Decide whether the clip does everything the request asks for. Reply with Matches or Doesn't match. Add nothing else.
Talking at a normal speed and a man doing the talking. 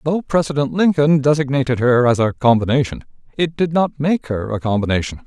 Matches